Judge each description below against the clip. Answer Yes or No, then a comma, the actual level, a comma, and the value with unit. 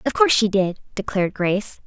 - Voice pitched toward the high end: Yes, high, 205 Hz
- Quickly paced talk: No, average, 195 wpm